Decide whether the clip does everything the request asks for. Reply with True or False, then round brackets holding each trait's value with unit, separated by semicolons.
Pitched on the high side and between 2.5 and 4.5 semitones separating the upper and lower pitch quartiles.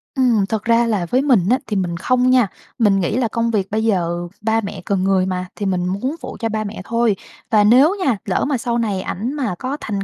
True (220 Hz; 3.7 semitones)